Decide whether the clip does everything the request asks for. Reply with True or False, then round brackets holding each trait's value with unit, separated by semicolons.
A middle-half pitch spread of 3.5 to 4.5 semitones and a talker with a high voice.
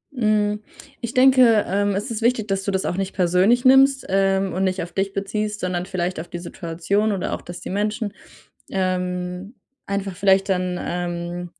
False (2.7 semitones; 195 Hz)